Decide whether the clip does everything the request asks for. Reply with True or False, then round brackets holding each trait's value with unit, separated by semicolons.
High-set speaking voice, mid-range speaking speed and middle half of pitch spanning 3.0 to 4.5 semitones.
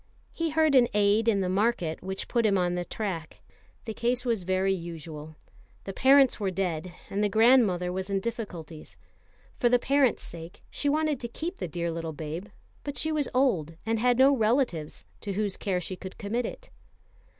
False (200 Hz; 190 wpm; 5.5 semitones)